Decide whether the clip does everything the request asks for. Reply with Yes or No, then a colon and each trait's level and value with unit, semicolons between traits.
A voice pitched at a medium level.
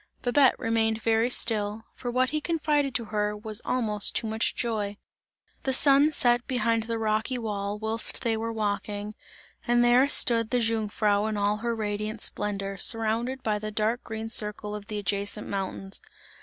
No: high, 220 Hz